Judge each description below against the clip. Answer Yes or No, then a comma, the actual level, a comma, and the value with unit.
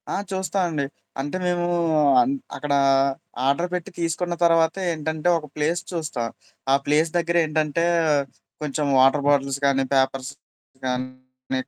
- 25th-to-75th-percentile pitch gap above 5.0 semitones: No, average, 3.8 semitones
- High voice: No, medium, 155 Hz